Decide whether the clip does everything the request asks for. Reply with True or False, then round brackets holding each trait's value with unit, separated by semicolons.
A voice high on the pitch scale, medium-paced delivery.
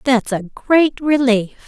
True (250 Hz; 145 wpm)